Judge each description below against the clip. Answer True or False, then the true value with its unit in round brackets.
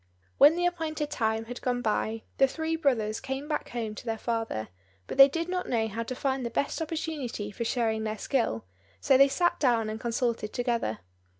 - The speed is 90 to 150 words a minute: False (200 wpm)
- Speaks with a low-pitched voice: False (245 Hz)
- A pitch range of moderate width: True (4.4 semitones)